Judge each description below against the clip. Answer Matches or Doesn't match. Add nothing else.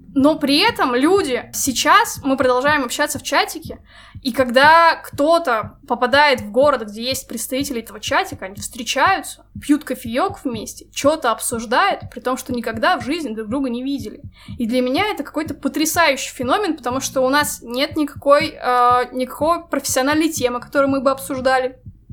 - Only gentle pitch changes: Doesn't match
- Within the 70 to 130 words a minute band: Doesn't match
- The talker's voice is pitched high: Matches